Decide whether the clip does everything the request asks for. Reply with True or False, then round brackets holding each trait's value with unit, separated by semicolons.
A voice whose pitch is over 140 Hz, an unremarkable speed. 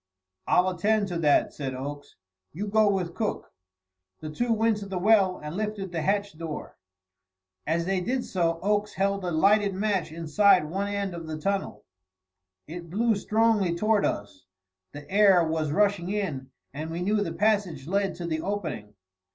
True (190 Hz; 170 wpm)